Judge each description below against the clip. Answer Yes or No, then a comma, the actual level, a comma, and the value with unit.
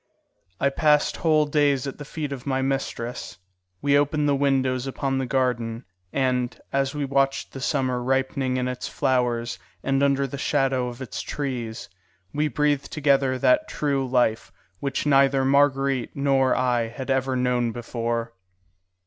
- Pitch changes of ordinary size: No, narrow, 1.9 semitones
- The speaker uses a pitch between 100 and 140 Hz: Yes, low, 135 Hz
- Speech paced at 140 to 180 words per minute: Yes, average, 155 wpm